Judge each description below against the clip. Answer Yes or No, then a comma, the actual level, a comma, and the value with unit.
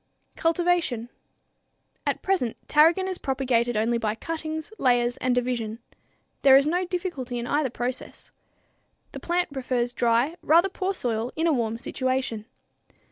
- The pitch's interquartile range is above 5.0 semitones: Yes, wide, 5.5 semitones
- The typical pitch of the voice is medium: No, very high, 260 Hz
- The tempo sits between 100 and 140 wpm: Yes, slow, 135 wpm